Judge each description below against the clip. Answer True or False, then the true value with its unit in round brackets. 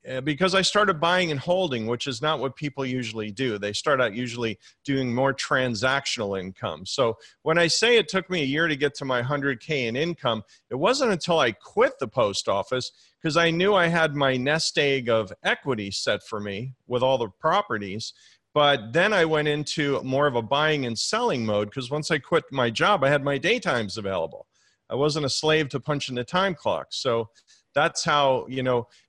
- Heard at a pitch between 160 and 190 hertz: False (135 Hz)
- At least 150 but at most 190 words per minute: False (205 wpm)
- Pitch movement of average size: True (4.5 semitones)